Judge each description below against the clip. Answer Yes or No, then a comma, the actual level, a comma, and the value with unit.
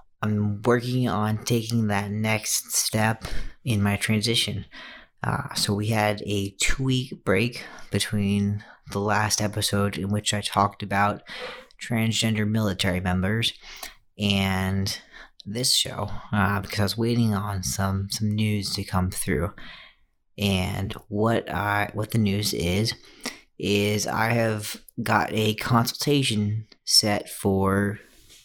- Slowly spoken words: Yes, slow, 125 wpm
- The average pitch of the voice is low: Yes, low, 105 Hz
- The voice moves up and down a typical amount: No, narrow, 1.7 semitones